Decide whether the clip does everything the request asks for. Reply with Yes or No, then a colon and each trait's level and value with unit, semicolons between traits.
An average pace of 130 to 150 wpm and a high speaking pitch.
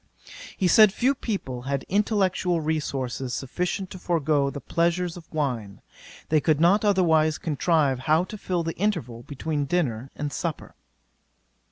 No: average, 145 wpm; medium, 160 Hz